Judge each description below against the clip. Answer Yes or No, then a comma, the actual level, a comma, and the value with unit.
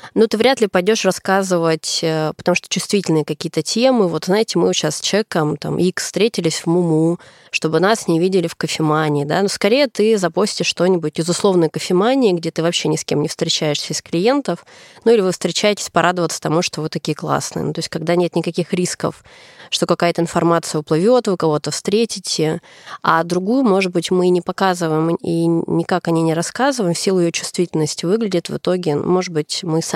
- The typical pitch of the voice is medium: Yes, medium, 175 Hz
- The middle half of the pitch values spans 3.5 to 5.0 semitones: No, average, 2.9 semitones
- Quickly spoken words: Yes, fast, 190 wpm